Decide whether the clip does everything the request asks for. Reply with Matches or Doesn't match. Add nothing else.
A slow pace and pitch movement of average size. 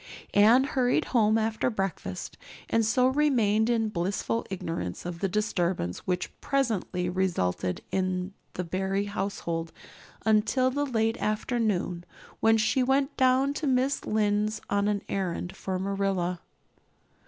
Matches